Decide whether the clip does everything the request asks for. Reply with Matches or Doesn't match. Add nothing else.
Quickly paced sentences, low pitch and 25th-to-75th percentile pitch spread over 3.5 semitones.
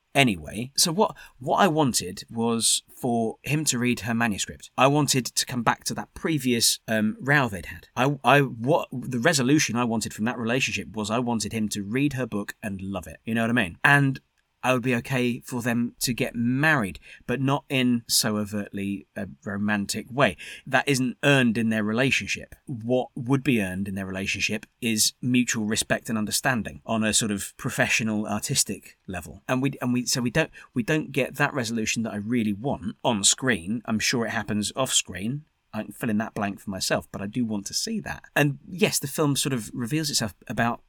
Matches